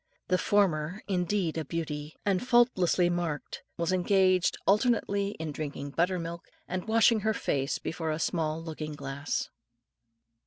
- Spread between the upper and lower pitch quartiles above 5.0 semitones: No, average, 4.1 semitones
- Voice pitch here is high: No, medium, 175 Hz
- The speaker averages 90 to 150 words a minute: Yes, average, 140 wpm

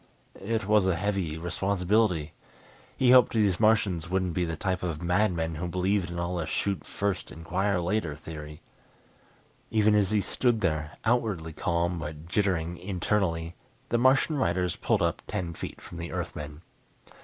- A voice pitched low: Yes, very low, 90 Hz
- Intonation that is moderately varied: Yes, average, 3.9 semitones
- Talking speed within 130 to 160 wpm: Yes, average, 155 wpm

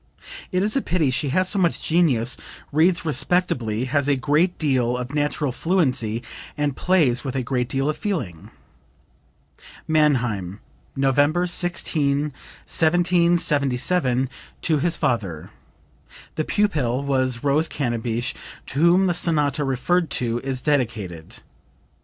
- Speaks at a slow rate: Yes, slow, 125 wpm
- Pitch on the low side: No, medium, 145 Hz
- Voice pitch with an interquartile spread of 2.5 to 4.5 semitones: No, average, 5.2 semitones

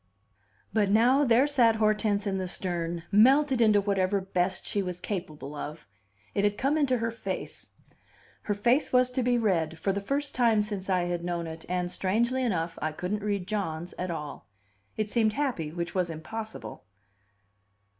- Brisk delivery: No, average, 175 wpm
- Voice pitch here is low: No, high, 200 Hz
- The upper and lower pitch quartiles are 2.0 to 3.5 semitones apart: No, average, 4.7 semitones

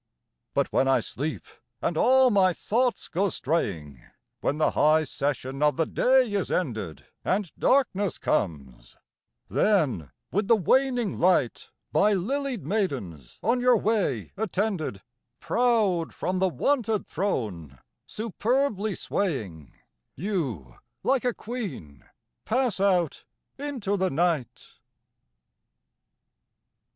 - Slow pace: Yes, slow, 110 wpm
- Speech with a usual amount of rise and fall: No, wide, 8.5 semitones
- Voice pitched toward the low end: No, medium, 185 Hz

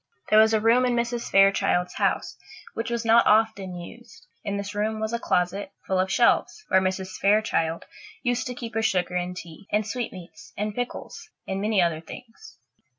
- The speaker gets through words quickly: No, average, 185 wpm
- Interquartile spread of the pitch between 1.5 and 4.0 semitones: Yes, average, 3.6 semitones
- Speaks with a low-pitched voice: No, high, 210 Hz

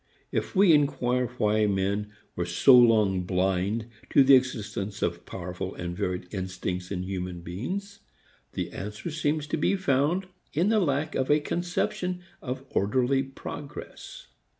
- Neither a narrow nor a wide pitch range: No, wide, 7.6 semitones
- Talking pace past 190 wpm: No, average, 145 wpm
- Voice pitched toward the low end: Yes, low, 120 Hz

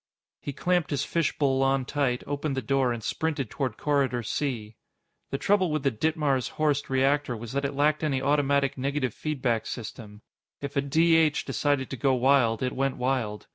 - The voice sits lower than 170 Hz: Yes, low, 135 Hz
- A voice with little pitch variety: Yes, narrow, 2.3 semitones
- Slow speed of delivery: No, average, 180 wpm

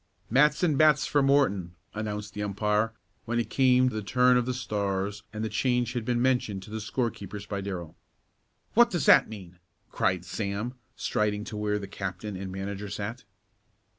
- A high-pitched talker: No, low, 105 Hz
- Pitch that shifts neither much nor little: Yes, average, 3.9 semitones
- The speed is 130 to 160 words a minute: No, average, 175 wpm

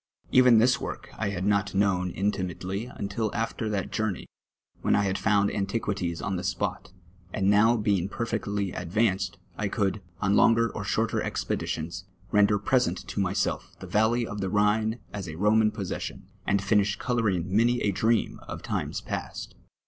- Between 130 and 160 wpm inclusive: No, average, 170 wpm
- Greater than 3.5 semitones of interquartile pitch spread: No, narrow, 2.4 semitones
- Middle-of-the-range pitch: No, low, 100 Hz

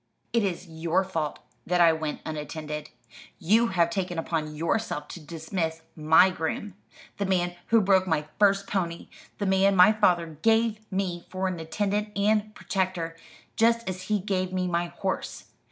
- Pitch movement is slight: No, average, 3.4 semitones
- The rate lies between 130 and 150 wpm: No, average, 160 wpm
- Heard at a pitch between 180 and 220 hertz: Yes, medium, 185 Hz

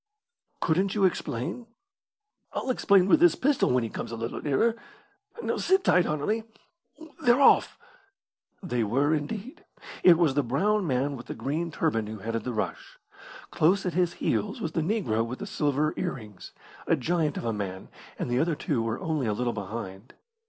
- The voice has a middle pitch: Yes, medium, 145 Hz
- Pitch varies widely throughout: Yes, wide, 7.9 semitones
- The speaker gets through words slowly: No, average, 180 wpm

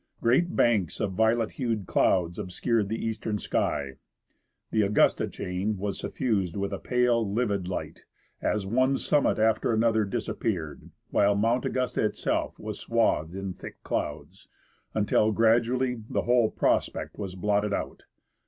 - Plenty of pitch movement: No, average, 3.0 semitones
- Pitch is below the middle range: Yes, low, 110 Hz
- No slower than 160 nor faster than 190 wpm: No, average, 140 wpm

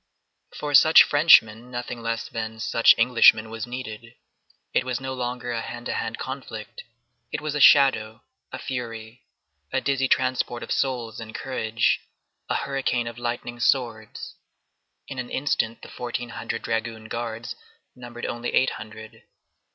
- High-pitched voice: No, low, 120 Hz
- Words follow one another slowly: No, average, 150 wpm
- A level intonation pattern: Yes, narrow, 2.2 semitones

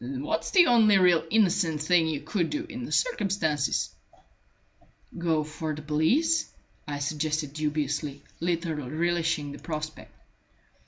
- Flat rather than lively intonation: No, average, 3.5 semitones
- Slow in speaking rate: Yes, slow, 125 wpm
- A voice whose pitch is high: No, medium, 160 Hz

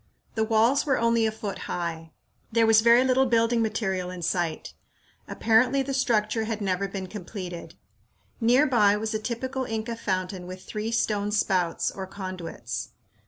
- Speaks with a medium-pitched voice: No, high, 215 Hz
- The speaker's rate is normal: Yes, average, 160 wpm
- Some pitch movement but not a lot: Yes, average, 3.7 semitones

